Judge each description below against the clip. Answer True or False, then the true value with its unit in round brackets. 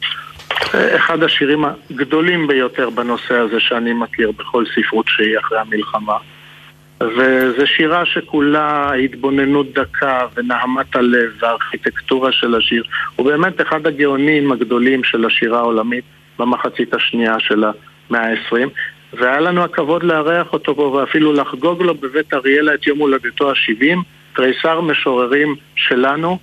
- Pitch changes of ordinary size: True (3.8 semitones)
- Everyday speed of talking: True (125 wpm)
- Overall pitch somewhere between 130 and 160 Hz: True (135 Hz)